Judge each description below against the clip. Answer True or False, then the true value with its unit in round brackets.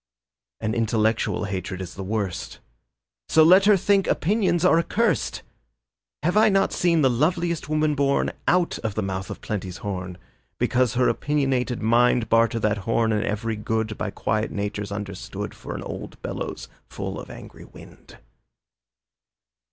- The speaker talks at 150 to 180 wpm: True (155 wpm)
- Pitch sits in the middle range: False (115 Hz)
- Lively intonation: True (7.3 semitones)